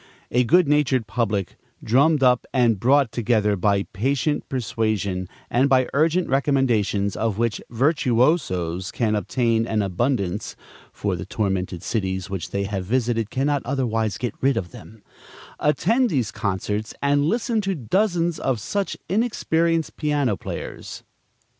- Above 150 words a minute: No, slow, 135 wpm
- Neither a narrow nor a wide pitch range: No, wide, 5.7 semitones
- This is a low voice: Yes, low, 120 Hz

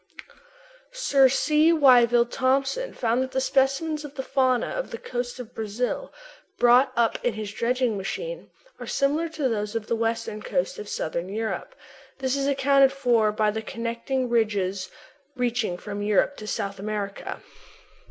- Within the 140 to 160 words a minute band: Yes, average, 155 wpm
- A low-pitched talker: No, high, 245 Hz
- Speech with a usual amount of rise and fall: Yes, average, 4.1 semitones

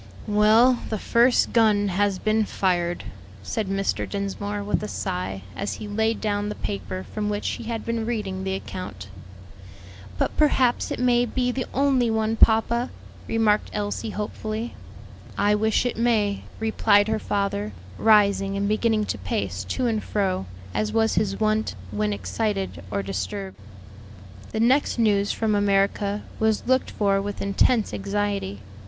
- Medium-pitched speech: No, high, 210 Hz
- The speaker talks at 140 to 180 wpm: Yes, average, 150 wpm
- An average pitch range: No, narrow, 2.2 semitones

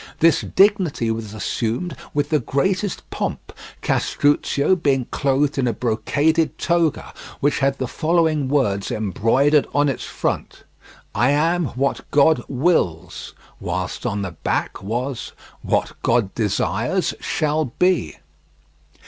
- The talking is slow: Yes, slow, 125 wpm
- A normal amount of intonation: No, wide, 5.7 semitones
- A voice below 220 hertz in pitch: Yes, medium, 140 Hz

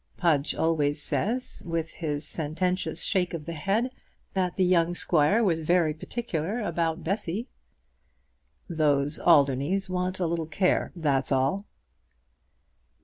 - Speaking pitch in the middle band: Yes, medium, 170 Hz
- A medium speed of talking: No, slow, 125 wpm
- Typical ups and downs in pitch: Yes, average, 3.4 semitones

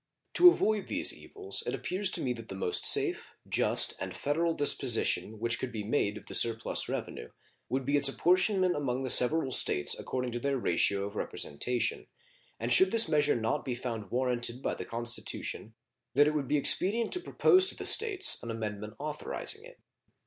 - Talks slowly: No, average, 185 wpm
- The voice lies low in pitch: Yes, low, 130 Hz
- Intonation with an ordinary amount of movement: No, wide, 7.0 semitones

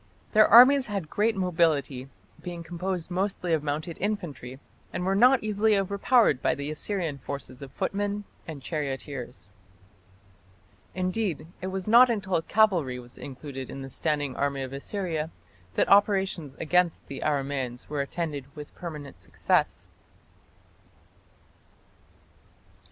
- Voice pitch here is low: No, medium, 165 Hz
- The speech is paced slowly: Yes, slow, 125 wpm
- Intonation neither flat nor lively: No, wide, 5.9 semitones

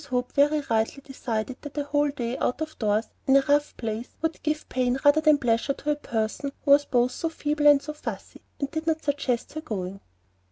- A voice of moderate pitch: No, very high, 280 Hz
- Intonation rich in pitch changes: No, average, 3.4 semitones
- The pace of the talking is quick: Yes, fast, 215 wpm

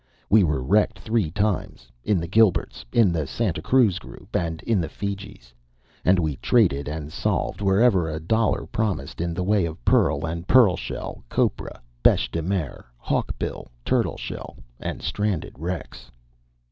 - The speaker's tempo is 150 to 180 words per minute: Yes, average, 160 wpm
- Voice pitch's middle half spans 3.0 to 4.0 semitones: No, average, 4.6 semitones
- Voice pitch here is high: No, very low, 90 Hz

